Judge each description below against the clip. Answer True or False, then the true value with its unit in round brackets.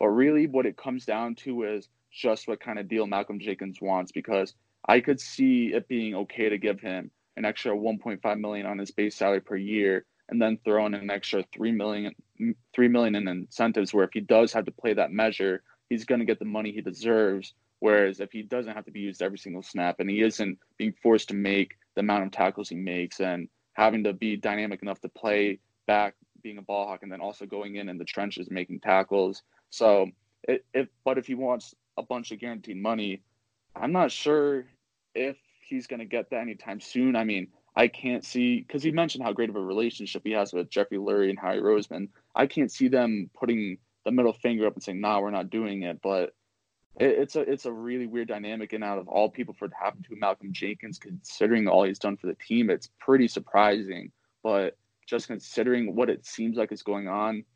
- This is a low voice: True (105 Hz)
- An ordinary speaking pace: False (225 wpm)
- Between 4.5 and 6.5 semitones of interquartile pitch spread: False (2.9 semitones)